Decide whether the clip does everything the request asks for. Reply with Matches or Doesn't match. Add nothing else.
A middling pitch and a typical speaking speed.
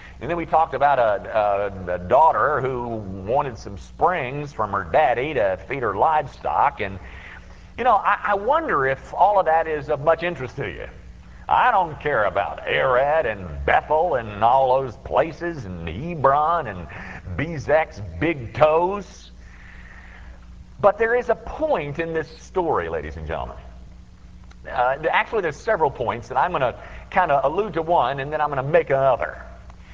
Doesn't match